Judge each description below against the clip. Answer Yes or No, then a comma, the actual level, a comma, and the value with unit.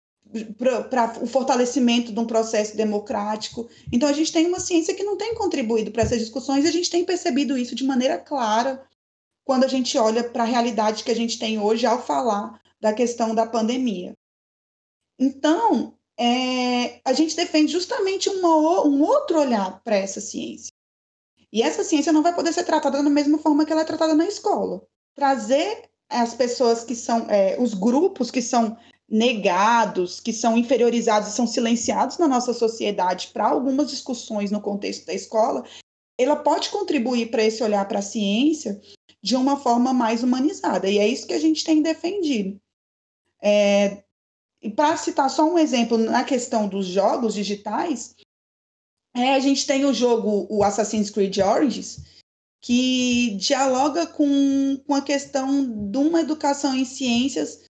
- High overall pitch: Yes, very high, 250 Hz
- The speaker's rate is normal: Yes, average, 165 wpm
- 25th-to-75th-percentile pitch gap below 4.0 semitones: No, average, 4.6 semitones